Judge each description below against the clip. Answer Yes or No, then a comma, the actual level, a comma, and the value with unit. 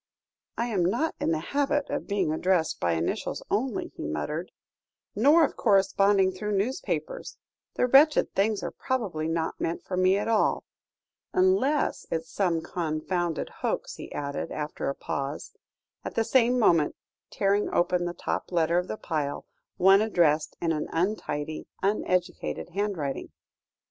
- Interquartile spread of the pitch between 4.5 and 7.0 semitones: Yes, average, 5.1 semitones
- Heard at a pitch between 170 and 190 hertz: Yes, medium, 185 Hz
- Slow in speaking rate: No, average, 150 wpm